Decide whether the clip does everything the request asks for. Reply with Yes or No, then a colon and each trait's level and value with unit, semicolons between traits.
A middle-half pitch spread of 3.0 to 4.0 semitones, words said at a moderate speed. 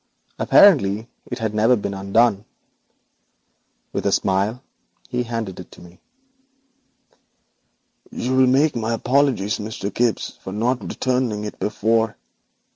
No: average, 3.3 semitones; slow, 125 wpm